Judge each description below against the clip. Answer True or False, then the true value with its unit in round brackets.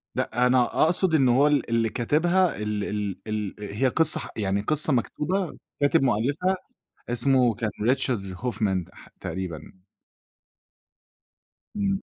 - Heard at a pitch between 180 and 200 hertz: False (120 Hz)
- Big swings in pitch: True (6.1 semitones)